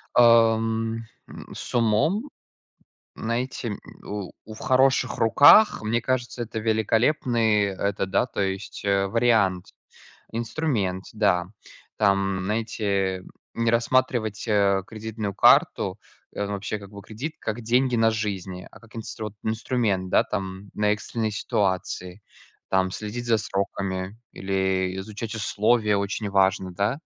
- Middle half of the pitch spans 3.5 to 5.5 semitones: No, average, 2.8 semitones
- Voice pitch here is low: Yes, low, 105 Hz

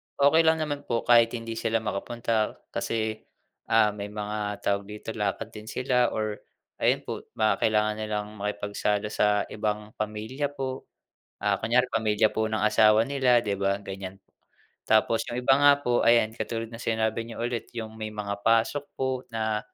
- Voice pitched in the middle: No, low, 110 Hz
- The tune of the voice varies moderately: No, narrow, 1.9 semitones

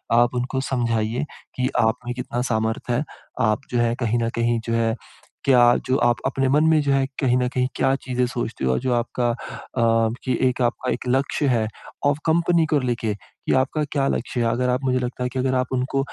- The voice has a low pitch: Yes, low, 125 Hz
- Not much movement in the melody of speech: Yes, narrow, 2.0 semitones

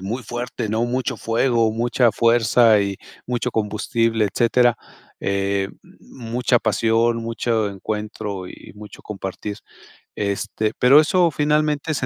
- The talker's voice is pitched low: Yes, low, 115 Hz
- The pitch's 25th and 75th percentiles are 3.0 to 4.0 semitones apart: No, narrow, 2.6 semitones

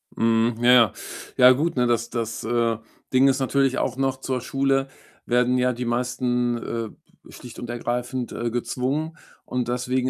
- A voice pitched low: Yes, low, 125 Hz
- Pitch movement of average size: No, narrow, 1.5 semitones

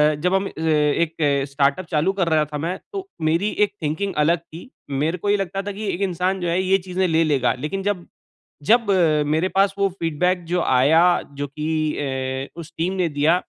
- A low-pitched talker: No, medium, 170 Hz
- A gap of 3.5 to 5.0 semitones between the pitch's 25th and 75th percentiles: Yes, average, 4.0 semitones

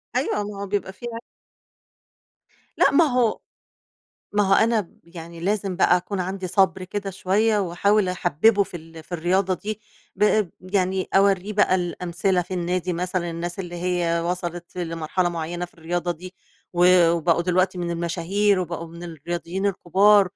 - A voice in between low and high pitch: Yes, medium, 180 Hz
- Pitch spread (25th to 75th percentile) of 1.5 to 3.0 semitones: Yes, narrow, 2.4 semitones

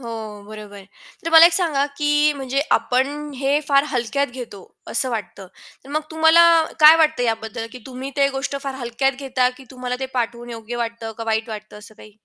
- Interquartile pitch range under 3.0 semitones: No, average, 3.9 semitones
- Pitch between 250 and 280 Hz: Yes, very high, 255 Hz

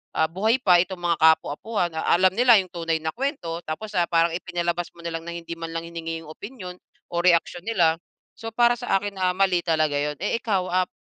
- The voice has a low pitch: No, medium, 175 Hz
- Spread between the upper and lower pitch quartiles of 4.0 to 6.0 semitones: No, average, 3.0 semitones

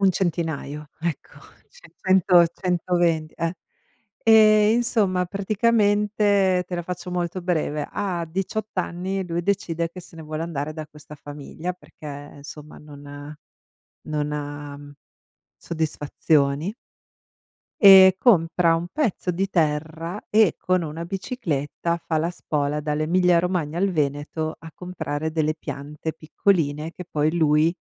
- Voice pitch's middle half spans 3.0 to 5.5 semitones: Yes, average, 3.5 semitones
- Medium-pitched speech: Yes, medium, 170 Hz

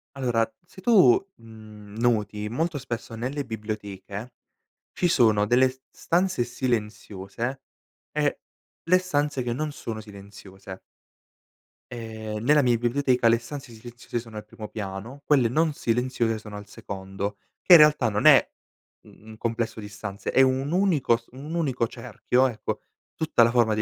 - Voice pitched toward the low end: Yes, low, 120 Hz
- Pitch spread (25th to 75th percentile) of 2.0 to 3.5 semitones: No, average, 4.0 semitones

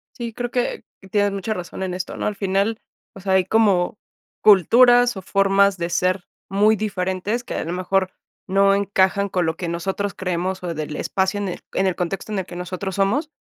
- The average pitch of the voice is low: No, high, 195 Hz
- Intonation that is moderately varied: No, narrow, 2.0 semitones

